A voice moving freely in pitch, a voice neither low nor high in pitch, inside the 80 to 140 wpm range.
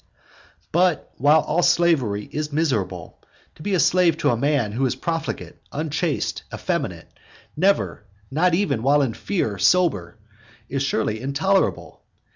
Yes: wide, 6.1 semitones; medium, 150 Hz; slow, 135 wpm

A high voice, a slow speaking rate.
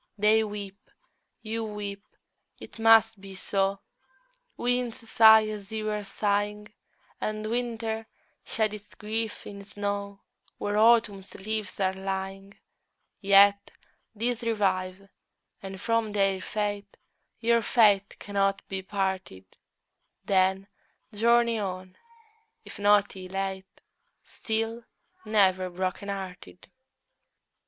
Yes: high, 205 Hz; slow, 105 wpm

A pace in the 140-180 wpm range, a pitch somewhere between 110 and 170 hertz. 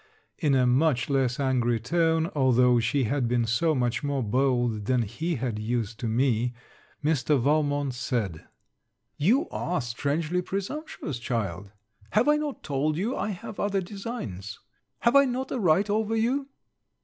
Yes: average, 155 wpm; medium, 140 Hz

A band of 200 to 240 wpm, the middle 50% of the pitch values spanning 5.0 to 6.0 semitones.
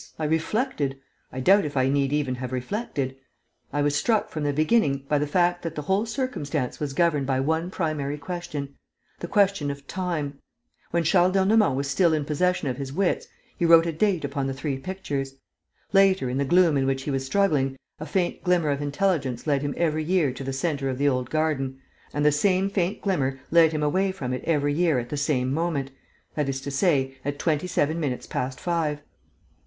No: fast, 205 wpm; average, 4.2 semitones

